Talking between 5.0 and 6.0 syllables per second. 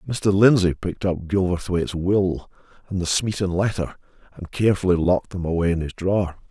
Yes: 5.7 syllables/s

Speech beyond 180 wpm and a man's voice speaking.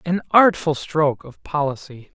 No: slow, 135 wpm; male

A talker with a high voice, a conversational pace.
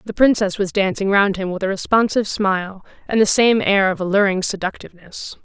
Yes: high, 200 Hz; average, 190 wpm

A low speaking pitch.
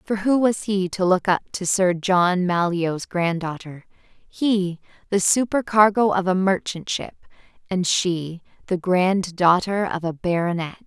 No: medium, 185 Hz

